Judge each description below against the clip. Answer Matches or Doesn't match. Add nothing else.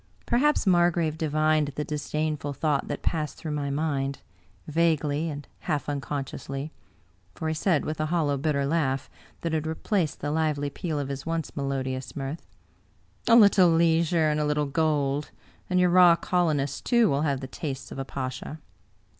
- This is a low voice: Doesn't match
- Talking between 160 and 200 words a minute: Matches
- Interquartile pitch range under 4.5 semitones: Matches